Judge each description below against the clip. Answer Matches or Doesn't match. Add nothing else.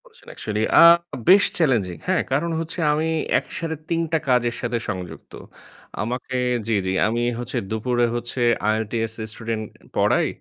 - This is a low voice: Matches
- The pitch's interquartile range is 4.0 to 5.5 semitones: Matches